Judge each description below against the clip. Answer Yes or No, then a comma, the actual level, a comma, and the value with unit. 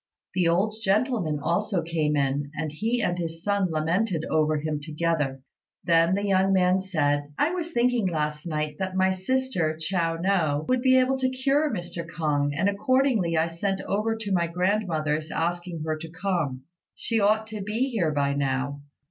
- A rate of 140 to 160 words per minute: No, average, 175 wpm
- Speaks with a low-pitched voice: No, medium, 175 Hz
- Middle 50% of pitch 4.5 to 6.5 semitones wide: Yes, average, 5.0 semitones